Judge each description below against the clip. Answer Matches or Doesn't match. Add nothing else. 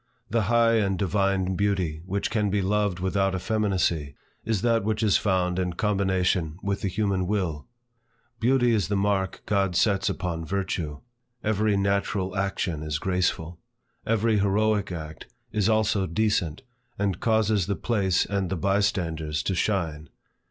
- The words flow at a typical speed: Matches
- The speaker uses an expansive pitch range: Doesn't match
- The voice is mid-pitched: Doesn't match